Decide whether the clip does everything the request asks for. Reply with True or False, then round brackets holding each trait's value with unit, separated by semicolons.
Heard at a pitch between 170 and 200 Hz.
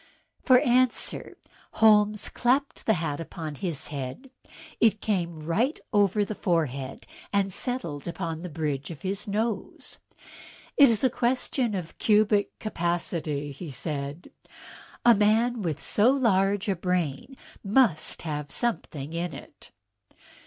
True (190 Hz)